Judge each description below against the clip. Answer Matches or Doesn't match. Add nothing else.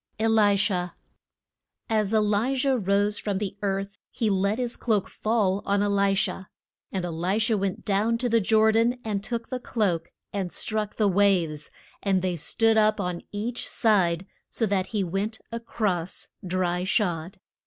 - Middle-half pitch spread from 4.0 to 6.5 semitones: Doesn't match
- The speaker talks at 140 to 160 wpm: Doesn't match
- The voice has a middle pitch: Doesn't match